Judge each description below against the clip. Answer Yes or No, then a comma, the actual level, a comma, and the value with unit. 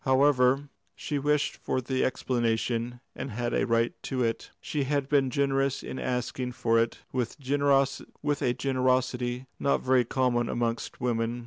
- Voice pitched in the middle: No, low, 130 Hz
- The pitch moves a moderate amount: No, narrow, 2.2 semitones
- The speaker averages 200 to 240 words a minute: No, average, 145 wpm